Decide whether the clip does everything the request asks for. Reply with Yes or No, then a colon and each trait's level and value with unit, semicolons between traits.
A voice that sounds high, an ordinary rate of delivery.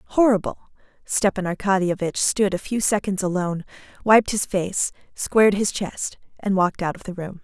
Yes: high, 195 Hz; average, 160 wpm